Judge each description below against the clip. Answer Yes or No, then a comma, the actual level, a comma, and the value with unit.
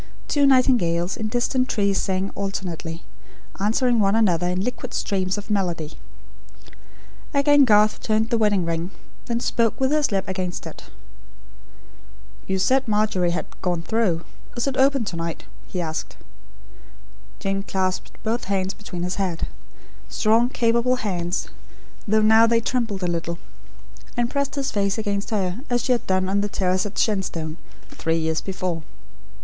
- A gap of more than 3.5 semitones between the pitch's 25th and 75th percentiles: Yes, average, 4.3 semitones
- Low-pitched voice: No, high, 200 Hz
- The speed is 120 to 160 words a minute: Yes, average, 155 wpm